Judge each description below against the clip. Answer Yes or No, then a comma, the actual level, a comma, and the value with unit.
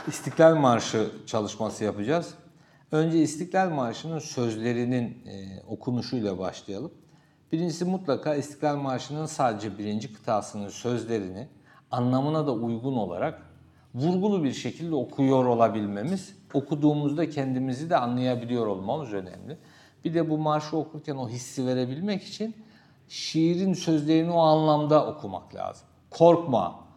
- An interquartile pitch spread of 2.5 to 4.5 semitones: No, average, 4.9 semitones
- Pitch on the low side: No, medium, 145 Hz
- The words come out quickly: No, average, 110 wpm